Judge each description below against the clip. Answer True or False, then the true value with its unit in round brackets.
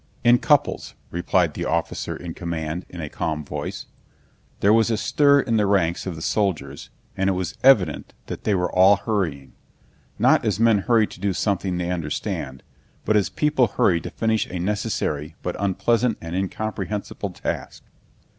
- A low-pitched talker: True (95 Hz)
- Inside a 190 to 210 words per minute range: False (165 wpm)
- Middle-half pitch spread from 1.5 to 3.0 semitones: False (4.3 semitones)